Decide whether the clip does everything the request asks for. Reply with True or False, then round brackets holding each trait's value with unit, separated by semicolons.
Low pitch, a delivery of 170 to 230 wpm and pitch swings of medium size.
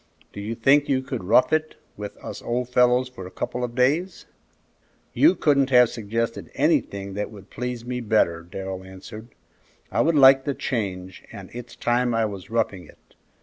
True (120 Hz; 180 wpm; 4.2 semitones)